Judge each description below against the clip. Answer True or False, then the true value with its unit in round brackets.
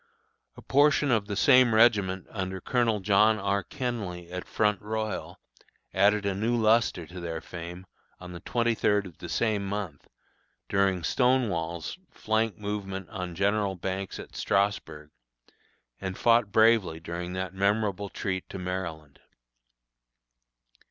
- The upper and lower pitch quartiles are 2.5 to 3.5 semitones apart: True (3.1 semitones)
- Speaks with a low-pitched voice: True (100 Hz)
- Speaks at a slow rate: True (130 wpm)